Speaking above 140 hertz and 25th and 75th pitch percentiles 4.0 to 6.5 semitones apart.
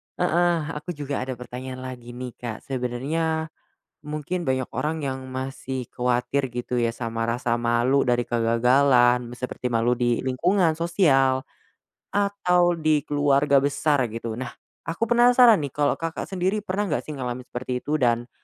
No: low, 130 Hz; average, 4.5 semitones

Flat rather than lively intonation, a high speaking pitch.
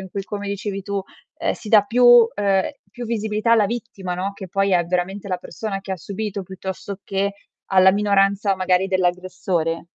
Yes: narrow, 1.7 semitones; high, 195 Hz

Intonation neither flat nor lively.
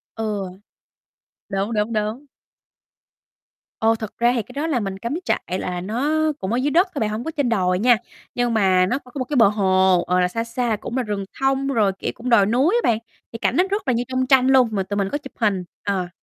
Yes: average, 4.4 semitones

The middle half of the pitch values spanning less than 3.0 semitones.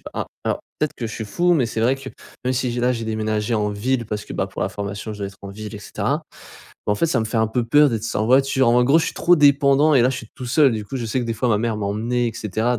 No: average, 3.6 semitones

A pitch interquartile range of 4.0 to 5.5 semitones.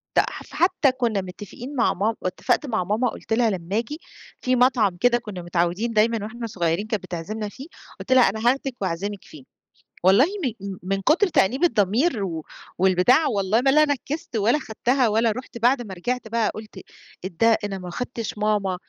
Yes: average, 4.4 semitones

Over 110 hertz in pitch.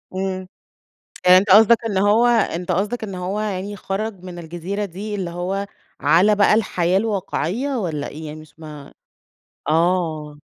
Yes: medium, 185 Hz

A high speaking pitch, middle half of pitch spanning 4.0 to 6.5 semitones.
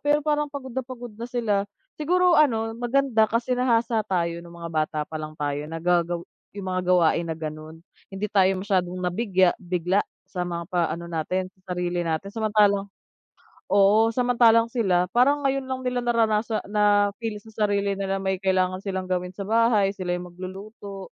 Yes: high, 200 Hz; average, 4.5 semitones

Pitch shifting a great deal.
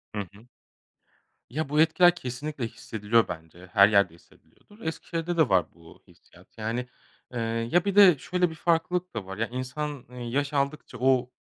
Yes: wide, 6.9 semitones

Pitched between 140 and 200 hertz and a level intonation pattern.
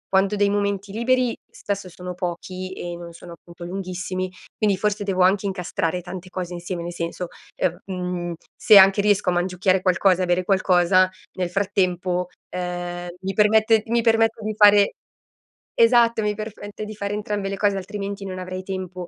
Yes: high, 190 Hz; narrow, 2.3 semitones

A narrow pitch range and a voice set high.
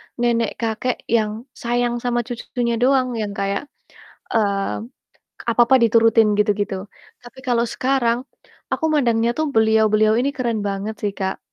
Yes: narrow, 2.2 semitones; high, 230 Hz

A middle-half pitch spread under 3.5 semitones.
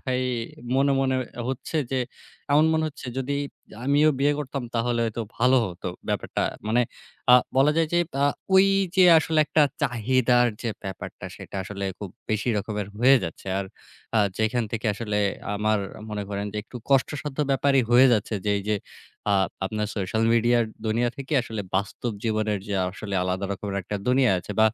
No: average, 4.3 semitones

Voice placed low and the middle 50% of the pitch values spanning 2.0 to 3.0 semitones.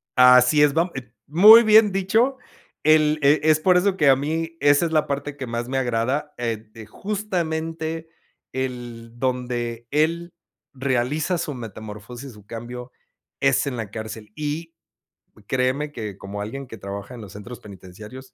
No: low, 130 Hz; average, 5.2 semitones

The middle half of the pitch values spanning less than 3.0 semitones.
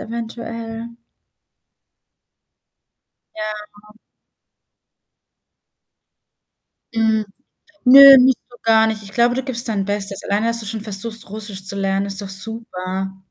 Yes: narrow, 2.6 semitones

